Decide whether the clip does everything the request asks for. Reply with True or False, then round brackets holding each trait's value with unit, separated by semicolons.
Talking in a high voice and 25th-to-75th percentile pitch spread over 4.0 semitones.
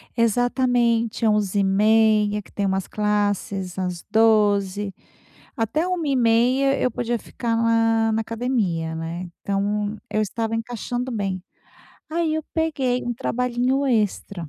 False (225 Hz; 3.2 semitones)